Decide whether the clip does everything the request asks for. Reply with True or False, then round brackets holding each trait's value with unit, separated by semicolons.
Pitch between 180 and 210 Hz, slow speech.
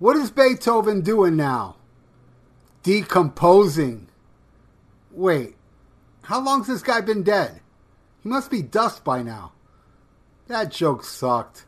True (190 Hz; 120 wpm)